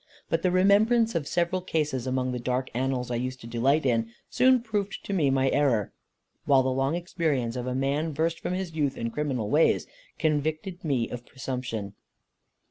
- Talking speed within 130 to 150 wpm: No, average, 185 wpm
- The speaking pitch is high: No, medium, 140 Hz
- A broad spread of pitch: No, average, 5.0 semitones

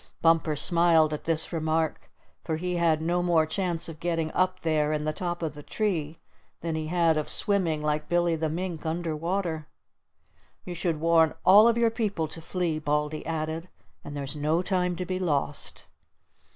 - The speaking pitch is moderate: Yes, medium, 165 Hz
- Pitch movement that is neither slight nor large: No, narrow, 2.2 semitones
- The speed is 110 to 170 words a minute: No, average, 180 wpm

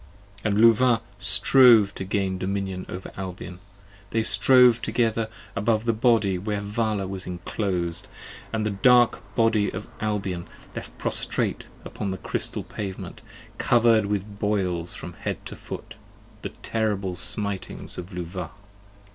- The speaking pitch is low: Yes, low, 100 Hz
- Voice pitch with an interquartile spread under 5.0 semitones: Yes, average, 2.9 semitones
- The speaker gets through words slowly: Yes, slow, 130 wpm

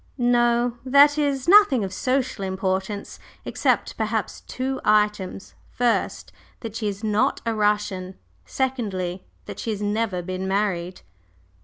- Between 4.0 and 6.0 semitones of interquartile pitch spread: Yes, average, 4.5 semitones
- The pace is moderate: No, slow, 130 wpm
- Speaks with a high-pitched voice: Yes, high, 215 Hz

